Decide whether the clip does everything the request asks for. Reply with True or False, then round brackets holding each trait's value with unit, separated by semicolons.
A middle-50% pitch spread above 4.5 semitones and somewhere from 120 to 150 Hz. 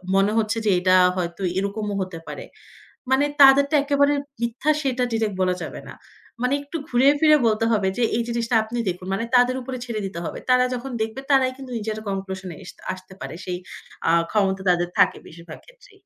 False (5.2 semitones; 225 Hz)